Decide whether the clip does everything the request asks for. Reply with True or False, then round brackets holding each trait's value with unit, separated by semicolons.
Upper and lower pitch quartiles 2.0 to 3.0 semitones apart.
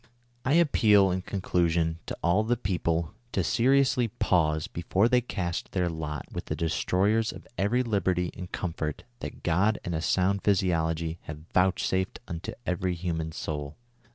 False (3.7 semitones)